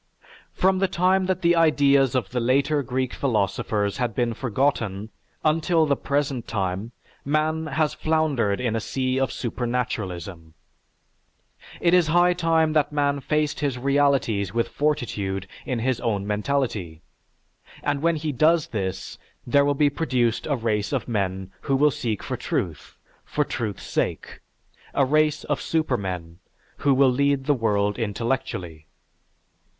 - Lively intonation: Yes, wide, 5.7 semitones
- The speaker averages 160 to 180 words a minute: No, average, 145 wpm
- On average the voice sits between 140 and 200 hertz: No, low, 130 Hz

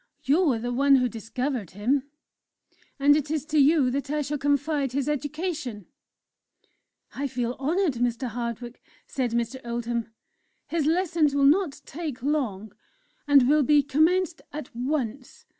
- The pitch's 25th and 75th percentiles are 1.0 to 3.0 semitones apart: No, average, 3.7 semitones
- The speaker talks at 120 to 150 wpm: Yes, average, 145 wpm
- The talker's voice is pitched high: Yes, very high, 275 Hz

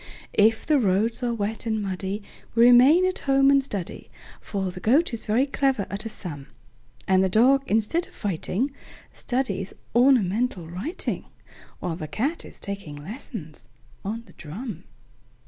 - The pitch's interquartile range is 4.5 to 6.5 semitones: Yes, wide, 5.6 semitones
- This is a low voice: No, high, 220 Hz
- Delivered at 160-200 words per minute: No, slow, 135 wpm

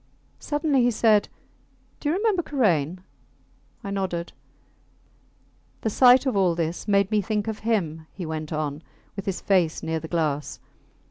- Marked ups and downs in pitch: Yes, wide, 5.8 semitones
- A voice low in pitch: No, high, 195 Hz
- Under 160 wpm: Yes, average, 150 wpm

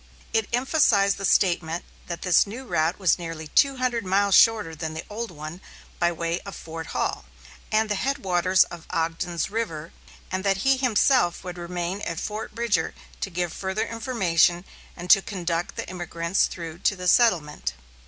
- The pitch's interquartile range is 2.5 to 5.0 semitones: Yes, average, 4.2 semitones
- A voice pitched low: No, medium, 185 Hz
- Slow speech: No, average, 170 wpm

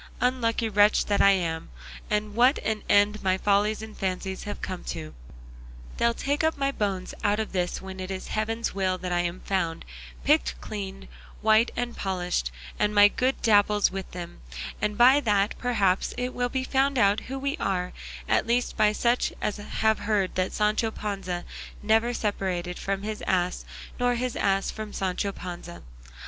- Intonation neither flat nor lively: Yes, average, 3.3 semitones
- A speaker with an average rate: Yes, average, 170 wpm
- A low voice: No, high, 205 Hz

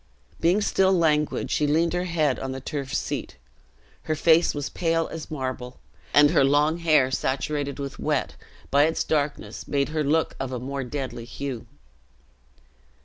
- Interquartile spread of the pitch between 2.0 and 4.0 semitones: Yes, average, 3.1 semitones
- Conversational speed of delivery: Yes, average, 160 wpm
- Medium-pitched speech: Yes, medium, 145 Hz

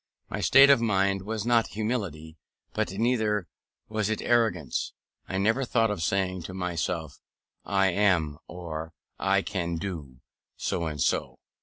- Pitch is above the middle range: No, very low, 95 Hz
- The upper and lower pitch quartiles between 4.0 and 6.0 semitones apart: Yes, average, 4.5 semitones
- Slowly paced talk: No, average, 145 wpm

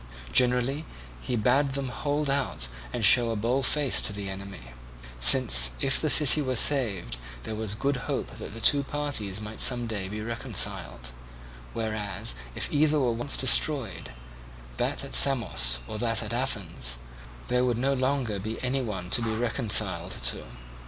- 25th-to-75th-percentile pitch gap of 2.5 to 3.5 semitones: No, average, 5.0 semitones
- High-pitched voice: No, low, 115 Hz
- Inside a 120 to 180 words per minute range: Yes, average, 165 wpm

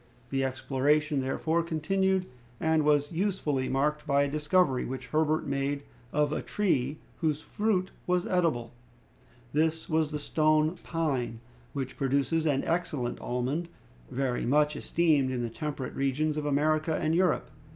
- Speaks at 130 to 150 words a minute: Yes, average, 140 wpm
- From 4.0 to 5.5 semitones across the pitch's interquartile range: No, average, 2.9 semitones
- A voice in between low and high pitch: Yes, medium, 150 Hz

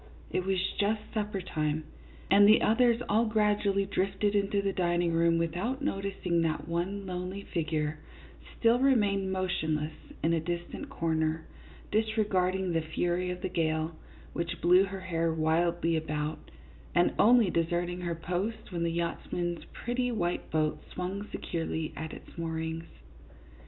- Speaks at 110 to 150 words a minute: Yes, average, 145 wpm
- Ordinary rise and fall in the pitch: Yes, average, 3.4 semitones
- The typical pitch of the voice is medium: Yes, medium, 180 Hz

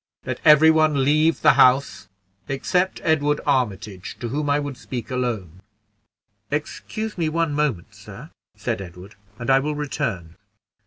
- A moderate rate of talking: Yes, average, 145 wpm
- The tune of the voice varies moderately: Yes, average, 4.3 semitones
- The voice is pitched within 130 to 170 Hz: Yes, medium, 140 Hz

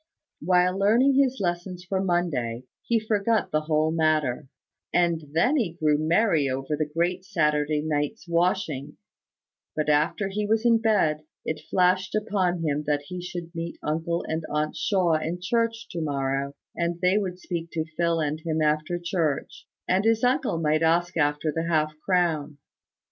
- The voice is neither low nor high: Yes, medium, 170 Hz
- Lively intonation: No, average, 3.6 semitones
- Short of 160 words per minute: No, average, 165 wpm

